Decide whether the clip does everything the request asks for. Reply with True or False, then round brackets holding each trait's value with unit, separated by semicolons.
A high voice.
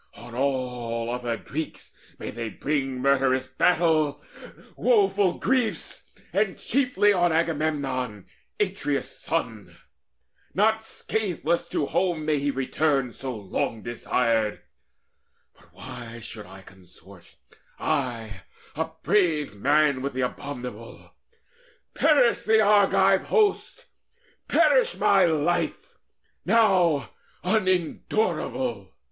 False (145 Hz)